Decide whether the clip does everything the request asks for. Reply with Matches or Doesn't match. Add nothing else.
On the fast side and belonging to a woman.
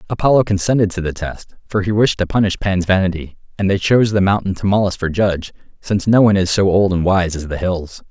Doesn't match